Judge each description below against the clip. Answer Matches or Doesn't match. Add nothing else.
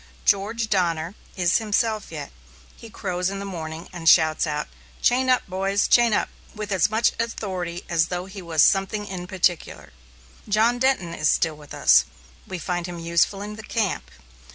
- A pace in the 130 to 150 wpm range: Doesn't match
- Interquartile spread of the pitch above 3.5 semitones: Matches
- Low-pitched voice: Doesn't match